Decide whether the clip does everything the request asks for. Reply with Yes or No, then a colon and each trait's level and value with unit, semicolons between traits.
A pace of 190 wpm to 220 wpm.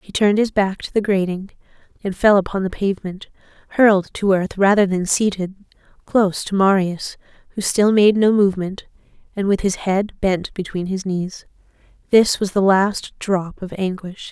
No: average, 170 wpm